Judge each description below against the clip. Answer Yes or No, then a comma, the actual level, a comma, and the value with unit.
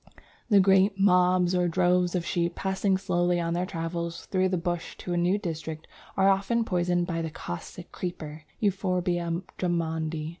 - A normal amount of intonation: No, narrow, 1.9 semitones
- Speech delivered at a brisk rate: No, average, 160 wpm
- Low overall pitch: No, medium, 180 Hz